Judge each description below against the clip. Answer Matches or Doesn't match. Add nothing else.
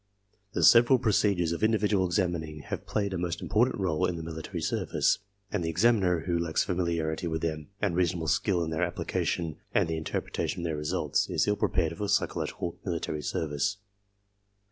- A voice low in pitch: Matches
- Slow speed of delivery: Doesn't match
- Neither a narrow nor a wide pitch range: Matches